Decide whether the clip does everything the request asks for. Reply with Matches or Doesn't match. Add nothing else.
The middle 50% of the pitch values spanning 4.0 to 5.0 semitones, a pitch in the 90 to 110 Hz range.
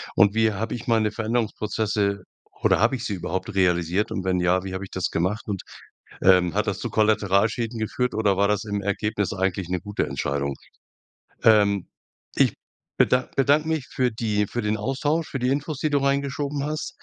Matches